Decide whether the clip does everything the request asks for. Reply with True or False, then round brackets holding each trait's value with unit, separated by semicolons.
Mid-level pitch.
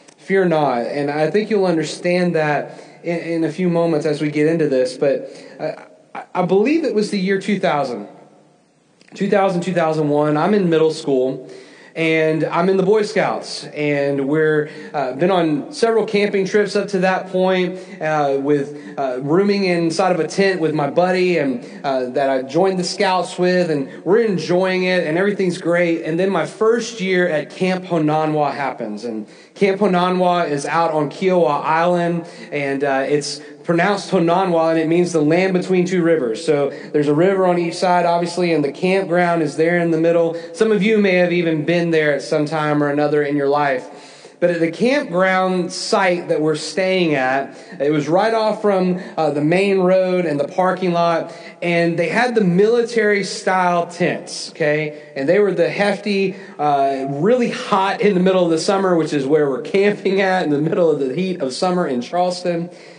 True (175 Hz)